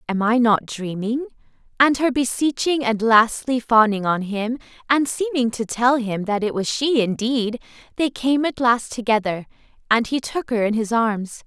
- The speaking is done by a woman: Yes, female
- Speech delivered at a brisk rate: No, average, 180 wpm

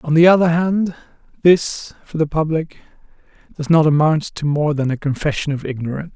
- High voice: No, medium, 155 Hz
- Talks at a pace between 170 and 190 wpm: Yes, average, 175 wpm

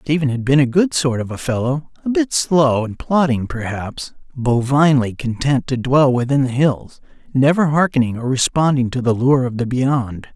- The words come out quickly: No, average, 185 wpm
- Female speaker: No, male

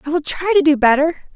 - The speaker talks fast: Yes, fast, 265 wpm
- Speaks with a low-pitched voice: No, very high, 310 Hz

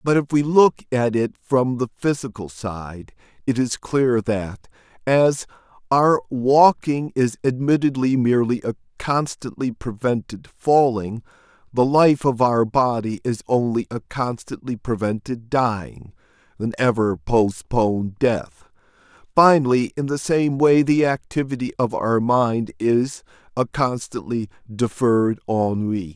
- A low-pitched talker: Yes, low, 125 Hz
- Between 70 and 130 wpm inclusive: Yes, slow, 125 wpm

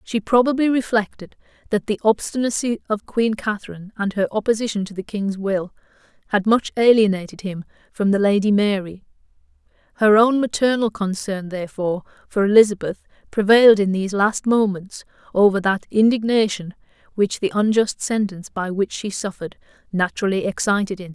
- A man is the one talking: No, female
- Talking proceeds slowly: No, average, 145 wpm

